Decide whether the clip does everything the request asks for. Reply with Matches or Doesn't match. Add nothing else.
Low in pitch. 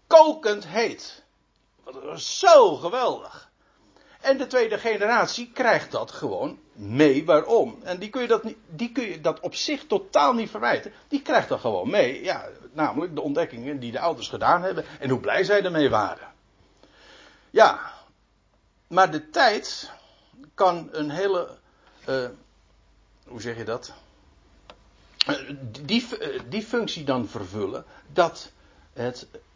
Doesn't match